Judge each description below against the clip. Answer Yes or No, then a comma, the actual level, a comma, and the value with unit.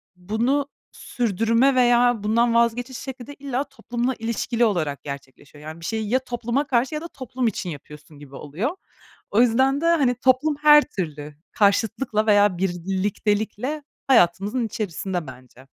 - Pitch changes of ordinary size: No, wide, 6.0 semitones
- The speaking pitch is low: No, high, 225 Hz